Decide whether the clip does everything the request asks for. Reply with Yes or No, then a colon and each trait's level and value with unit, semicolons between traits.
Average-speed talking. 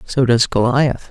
Yes: average, 160 wpm